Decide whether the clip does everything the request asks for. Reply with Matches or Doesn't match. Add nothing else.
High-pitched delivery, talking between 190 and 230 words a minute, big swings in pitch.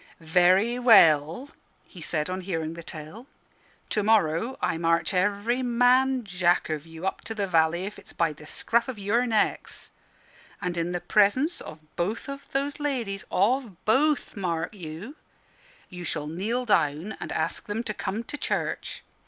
Doesn't match